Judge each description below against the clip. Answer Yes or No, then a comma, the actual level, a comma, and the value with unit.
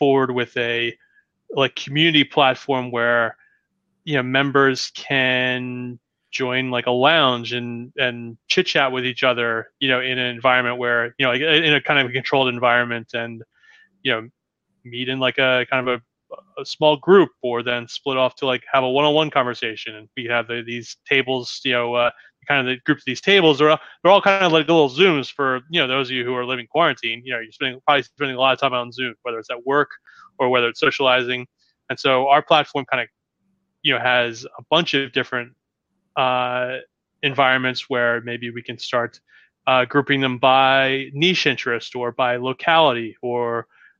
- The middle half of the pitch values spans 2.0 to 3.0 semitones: Yes, narrow, 2.5 semitones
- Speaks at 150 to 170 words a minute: No, average, 200 wpm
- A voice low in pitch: Yes, low, 130 Hz